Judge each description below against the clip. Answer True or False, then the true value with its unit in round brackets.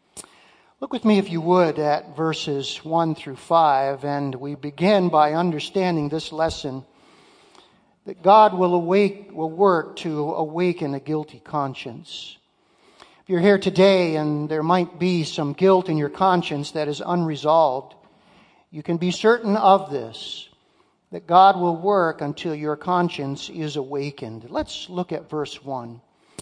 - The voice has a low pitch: False (160 Hz)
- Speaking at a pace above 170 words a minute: False (150 wpm)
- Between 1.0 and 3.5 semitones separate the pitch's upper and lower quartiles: False (3.9 semitones)